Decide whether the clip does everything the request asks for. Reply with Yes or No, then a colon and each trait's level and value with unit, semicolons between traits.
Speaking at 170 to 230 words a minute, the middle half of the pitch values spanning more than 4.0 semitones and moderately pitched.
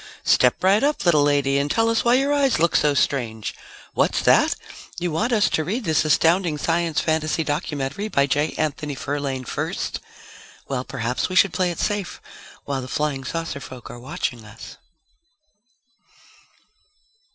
No: average, 160 wpm; average, 4.9 semitones; medium, 150 Hz